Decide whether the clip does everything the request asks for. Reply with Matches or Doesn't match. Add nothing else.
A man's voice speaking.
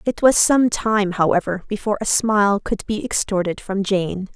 Doesn't match